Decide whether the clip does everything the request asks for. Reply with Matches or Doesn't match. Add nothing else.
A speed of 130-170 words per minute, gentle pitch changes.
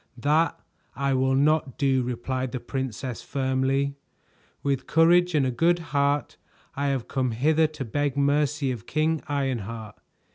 Matches